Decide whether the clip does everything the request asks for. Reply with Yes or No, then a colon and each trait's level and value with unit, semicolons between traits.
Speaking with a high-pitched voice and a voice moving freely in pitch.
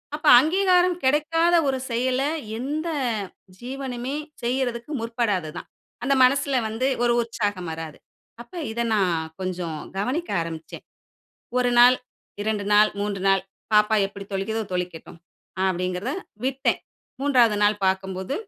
Yes: high, 230 Hz; wide, 5.8 semitones